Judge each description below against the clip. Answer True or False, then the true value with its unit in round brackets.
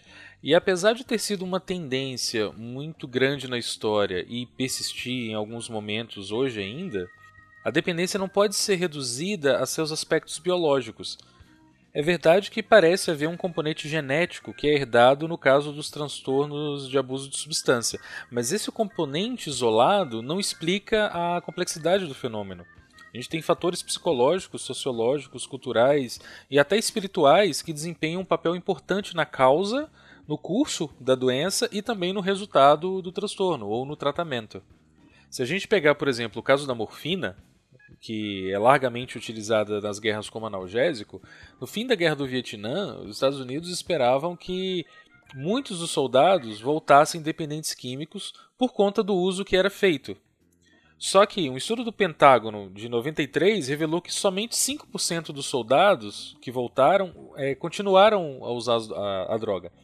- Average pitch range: False (7.4 semitones)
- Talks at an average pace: True (155 wpm)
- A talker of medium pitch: True (150 Hz)